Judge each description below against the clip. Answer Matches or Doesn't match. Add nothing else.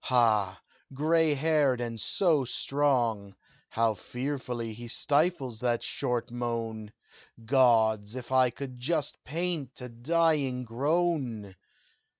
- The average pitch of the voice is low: Matches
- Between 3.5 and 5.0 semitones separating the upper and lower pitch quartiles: Matches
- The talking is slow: Matches